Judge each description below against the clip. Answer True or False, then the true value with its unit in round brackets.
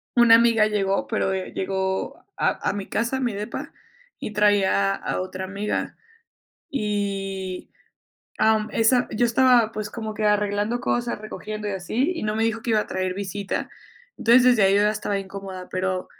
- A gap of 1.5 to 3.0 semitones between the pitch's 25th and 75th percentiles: True (2.7 semitones)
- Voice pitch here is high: True (210 Hz)